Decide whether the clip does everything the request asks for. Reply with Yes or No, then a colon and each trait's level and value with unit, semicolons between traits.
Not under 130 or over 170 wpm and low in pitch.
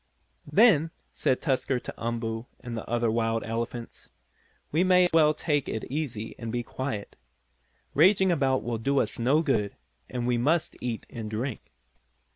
Yes: average, 160 wpm; low, 125 Hz